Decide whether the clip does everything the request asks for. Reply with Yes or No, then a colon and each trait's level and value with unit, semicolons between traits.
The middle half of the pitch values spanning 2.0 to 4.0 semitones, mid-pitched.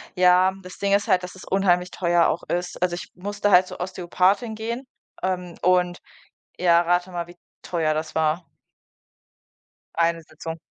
No: narrow, 1.5 semitones; medium, 180 Hz